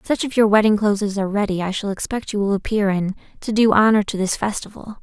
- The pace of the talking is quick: Yes, fast, 250 wpm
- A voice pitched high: Yes, high, 205 Hz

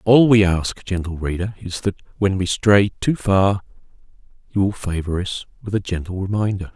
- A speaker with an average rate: Yes, average, 180 wpm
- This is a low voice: Yes, very low, 95 Hz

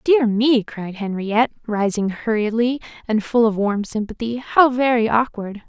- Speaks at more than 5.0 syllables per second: No, 4.5 syllables/s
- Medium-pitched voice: No, high, 225 Hz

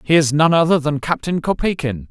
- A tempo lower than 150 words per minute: No, average, 200 wpm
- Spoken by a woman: No, male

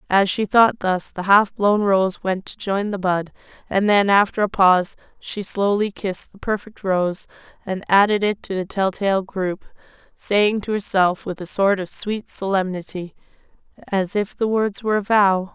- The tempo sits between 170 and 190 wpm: Yes, average, 185 wpm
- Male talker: No, female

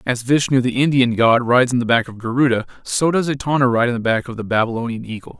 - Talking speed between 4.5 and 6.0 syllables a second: No, 6.5 syllables/s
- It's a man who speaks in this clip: Yes, male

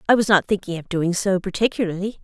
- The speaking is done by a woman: Yes, female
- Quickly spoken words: Yes, fast, 215 wpm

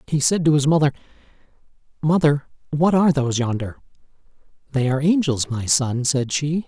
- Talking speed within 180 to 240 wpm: No, average, 155 wpm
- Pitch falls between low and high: Yes, medium, 145 Hz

